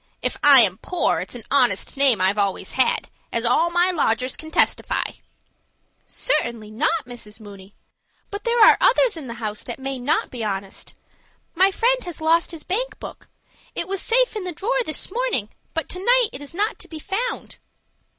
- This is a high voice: Yes, very high, 315 Hz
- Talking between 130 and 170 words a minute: No, average, 190 wpm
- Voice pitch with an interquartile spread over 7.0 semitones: Yes, wide, 9.0 semitones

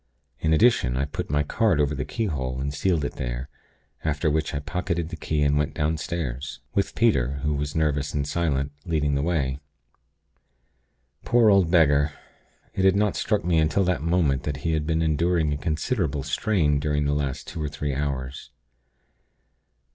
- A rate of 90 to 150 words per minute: No, average, 175 wpm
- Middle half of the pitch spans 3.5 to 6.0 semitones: No, average, 3.0 semitones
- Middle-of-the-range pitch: No, very low, 75 Hz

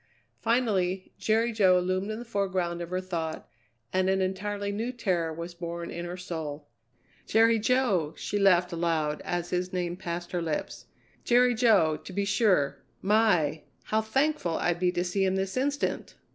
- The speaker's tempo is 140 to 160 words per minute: No, average, 170 wpm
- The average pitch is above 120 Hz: Yes, medium, 185 Hz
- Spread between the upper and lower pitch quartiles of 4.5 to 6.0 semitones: No, average, 3.9 semitones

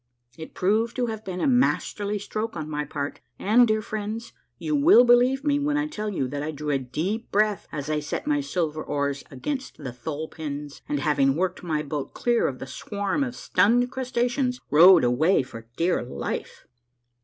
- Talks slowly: No, average, 190 wpm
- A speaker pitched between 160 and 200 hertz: Yes, high, 190 Hz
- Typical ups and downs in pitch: No, wide, 8.5 semitones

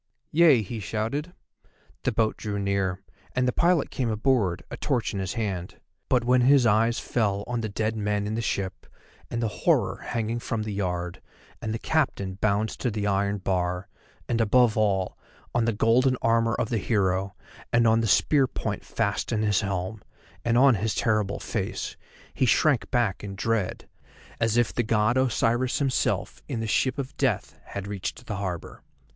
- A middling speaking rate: Yes, average, 180 wpm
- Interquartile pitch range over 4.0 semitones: No, average, 3.2 semitones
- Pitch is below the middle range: Yes, low, 110 Hz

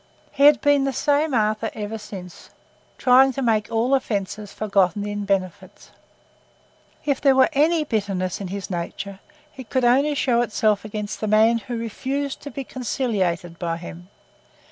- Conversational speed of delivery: Yes, average, 160 wpm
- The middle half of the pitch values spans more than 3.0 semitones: Yes, average, 5.1 semitones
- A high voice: Yes, high, 220 Hz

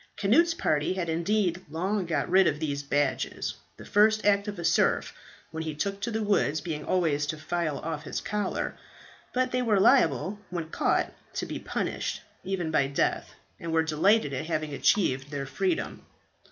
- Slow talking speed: No, average, 180 wpm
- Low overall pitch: No, medium, 170 Hz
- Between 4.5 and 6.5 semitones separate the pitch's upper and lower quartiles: Yes, average, 5.2 semitones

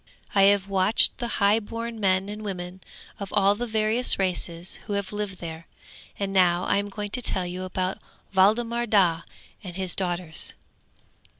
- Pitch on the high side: Yes, high, 195 Hz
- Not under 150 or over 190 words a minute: Yes, average, 165 wpm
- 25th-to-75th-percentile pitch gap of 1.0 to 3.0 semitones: Yes, narrow, 2.4 semitones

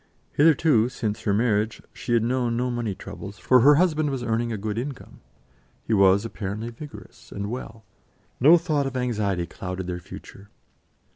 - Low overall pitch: Yes, low, 115 Hz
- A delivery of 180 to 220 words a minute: No, average, 165 wpm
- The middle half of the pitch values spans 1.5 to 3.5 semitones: No, average, 4.1 semitones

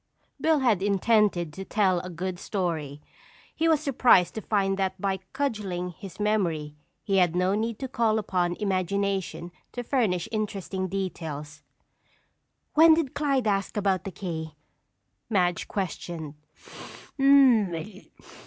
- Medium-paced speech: No, slow, 125 wpm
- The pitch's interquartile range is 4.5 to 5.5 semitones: No, average, 3.5 semitones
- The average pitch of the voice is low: No, high, 195 Hz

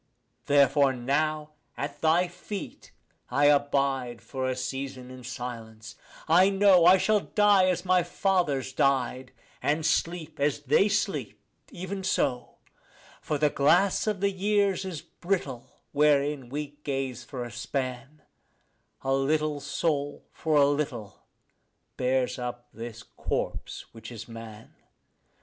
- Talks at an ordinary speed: No, slow, 130 wpm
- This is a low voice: No, medium, 145 Hz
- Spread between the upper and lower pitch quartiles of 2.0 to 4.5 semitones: No, average, 5.2 semitones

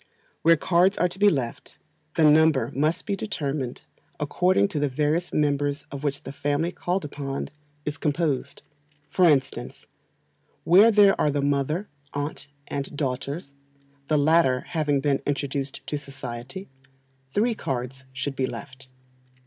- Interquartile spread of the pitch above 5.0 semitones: No, average, 3.4 semitones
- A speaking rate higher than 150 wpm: No, average, 140 wpm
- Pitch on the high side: No, medium, 145 Hz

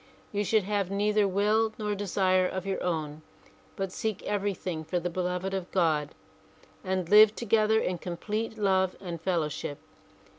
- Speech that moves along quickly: No, average, 155 wpm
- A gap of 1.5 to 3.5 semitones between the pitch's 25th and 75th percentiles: Yes, average, 2.8 semitones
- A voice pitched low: No, high, 190 Hz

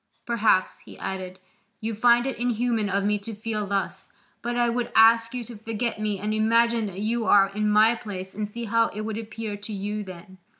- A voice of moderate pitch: No, high, 215 Hz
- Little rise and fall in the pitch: Yes, narrow, 2.1 semitones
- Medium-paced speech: No, fast, 210 wpm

